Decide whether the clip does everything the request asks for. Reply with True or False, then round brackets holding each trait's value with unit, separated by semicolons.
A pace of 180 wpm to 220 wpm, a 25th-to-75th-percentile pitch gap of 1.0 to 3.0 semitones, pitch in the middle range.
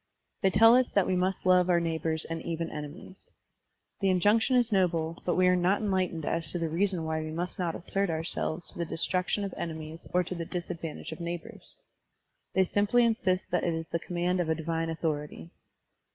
True (200 wpm; 2.4 semitones; 175 Hz)